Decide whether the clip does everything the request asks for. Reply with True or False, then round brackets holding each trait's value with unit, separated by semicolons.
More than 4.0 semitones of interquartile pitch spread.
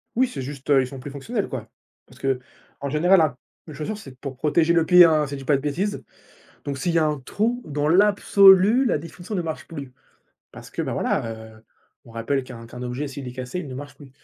True (4.9 semitones)